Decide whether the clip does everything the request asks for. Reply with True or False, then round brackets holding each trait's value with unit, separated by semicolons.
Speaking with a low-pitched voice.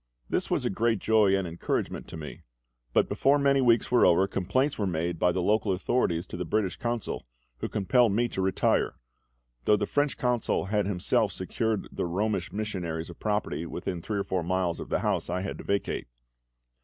True (100 Hz)